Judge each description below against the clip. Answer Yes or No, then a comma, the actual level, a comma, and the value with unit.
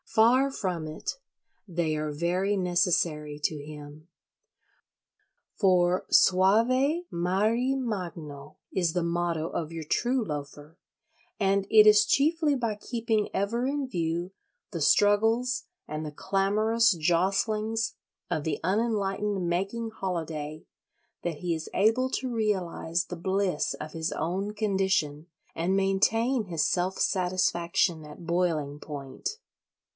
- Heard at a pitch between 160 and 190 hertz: Yes, medium, 185 Hz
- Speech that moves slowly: Yes, slow, 120 wpm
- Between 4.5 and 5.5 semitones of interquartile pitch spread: Yes, average, 5.0 semitones